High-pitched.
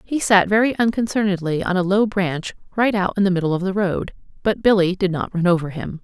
Yes: high, 195 Hz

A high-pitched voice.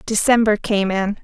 Yes: high, 210 Hz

